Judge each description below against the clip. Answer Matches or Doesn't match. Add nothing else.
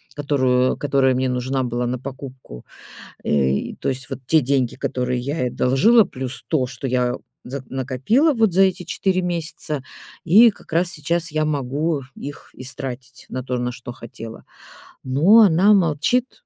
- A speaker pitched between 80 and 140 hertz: Matches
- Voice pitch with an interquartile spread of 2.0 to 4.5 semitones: Doesn't match